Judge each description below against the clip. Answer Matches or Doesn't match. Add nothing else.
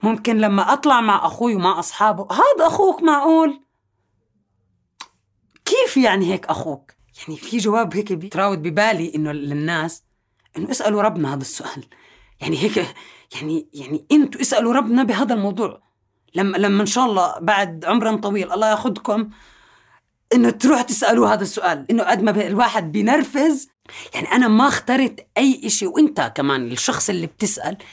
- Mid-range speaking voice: Doesn't match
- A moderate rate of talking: Doesn't match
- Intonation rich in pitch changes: Matches